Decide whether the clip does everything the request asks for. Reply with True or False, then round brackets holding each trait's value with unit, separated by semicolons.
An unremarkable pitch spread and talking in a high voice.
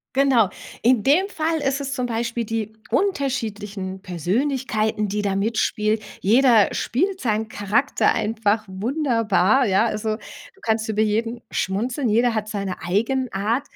True (3.8 semitones; 225 Hz)